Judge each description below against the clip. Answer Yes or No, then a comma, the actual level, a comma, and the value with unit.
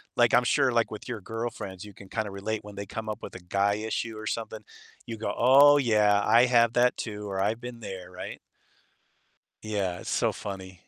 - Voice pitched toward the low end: Yes, low, 105 Hz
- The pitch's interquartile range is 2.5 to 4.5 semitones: Yes, average, 2.8 semitones